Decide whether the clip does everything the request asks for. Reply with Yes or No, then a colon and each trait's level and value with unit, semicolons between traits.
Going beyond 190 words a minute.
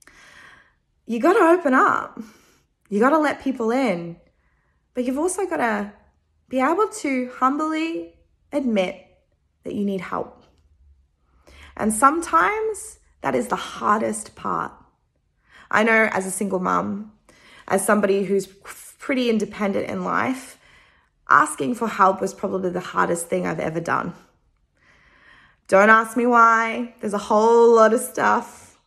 No: slow, 135 wpm